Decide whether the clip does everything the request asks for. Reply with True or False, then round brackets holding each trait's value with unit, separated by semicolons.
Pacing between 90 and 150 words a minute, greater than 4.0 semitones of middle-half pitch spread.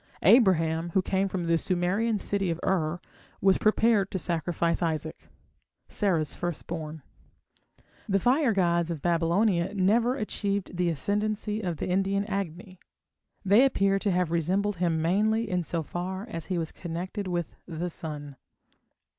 False (145 wpm; 3.2 semitones)